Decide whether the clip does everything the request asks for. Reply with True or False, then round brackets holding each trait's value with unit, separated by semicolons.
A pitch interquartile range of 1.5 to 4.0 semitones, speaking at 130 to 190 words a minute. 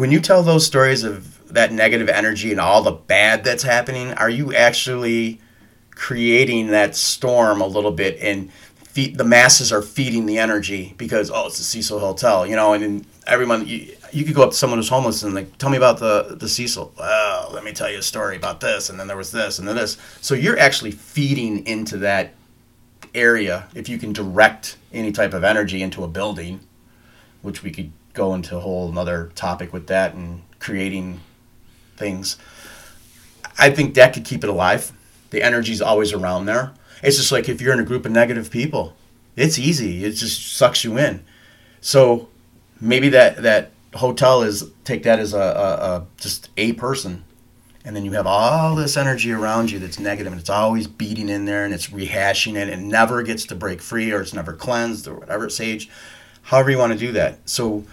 False (3.2 semitones; 205 wpm)